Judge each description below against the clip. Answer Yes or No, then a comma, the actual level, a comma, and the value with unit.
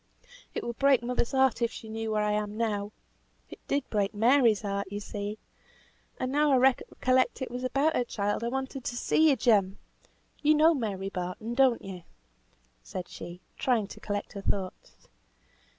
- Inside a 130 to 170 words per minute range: No, average, 180 wpm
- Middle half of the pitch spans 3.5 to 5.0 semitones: Yes, average, 4.2 semitones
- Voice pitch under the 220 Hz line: No, high, 230 Hz